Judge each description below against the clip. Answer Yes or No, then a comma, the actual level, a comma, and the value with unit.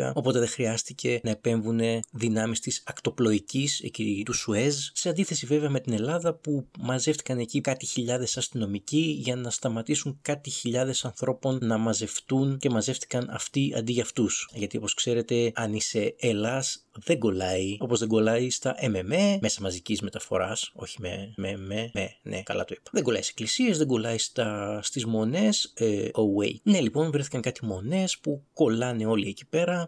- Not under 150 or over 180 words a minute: Yes, average, 165 wpm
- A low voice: Yes, low, 120 Hz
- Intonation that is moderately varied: Yes, average, 3.9 semitones